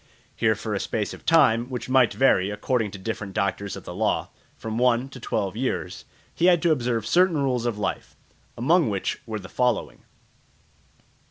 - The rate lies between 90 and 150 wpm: No, average, 180 wpm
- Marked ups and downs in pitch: No, average, 4.1 semitones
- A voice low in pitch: Yes, low, 120 Hz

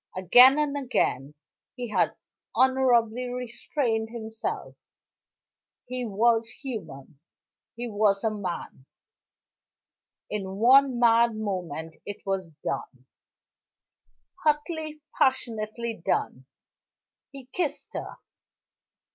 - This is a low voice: No, high, 230 Hz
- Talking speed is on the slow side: Yes, slow, 90 wpm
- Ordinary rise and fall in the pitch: Yes, average, 4.5 semitones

